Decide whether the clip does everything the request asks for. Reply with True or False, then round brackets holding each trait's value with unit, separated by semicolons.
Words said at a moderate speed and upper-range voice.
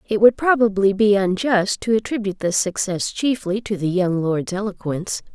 True (170 wpm; 205 Hz)